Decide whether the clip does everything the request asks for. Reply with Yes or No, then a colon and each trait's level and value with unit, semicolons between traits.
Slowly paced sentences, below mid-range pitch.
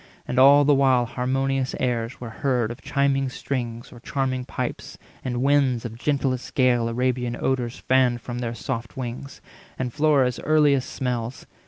No: average, 155 wpm; low, 130 Hz